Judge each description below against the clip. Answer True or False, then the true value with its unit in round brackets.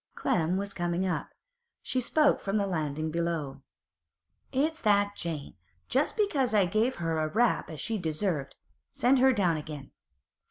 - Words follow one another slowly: False (155 wpm)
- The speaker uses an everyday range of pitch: False (6.1 semitones)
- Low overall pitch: False (185 Hz)